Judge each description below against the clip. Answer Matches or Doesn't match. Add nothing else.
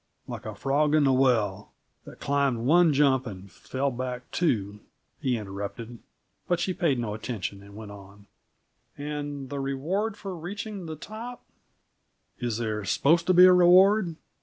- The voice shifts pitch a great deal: Matches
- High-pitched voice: Doesn't match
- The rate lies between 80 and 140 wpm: Doesn't match